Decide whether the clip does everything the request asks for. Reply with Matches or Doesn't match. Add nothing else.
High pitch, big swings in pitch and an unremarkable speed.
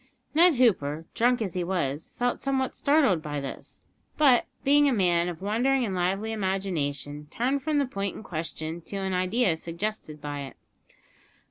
Matches